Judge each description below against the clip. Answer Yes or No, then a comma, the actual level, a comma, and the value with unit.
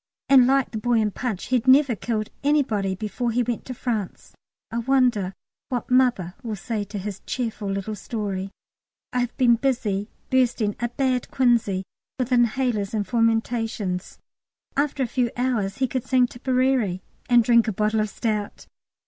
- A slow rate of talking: No, average, 165 wpm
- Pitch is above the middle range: Yes, high, 235 Hz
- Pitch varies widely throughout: No, average, 3.3 semitones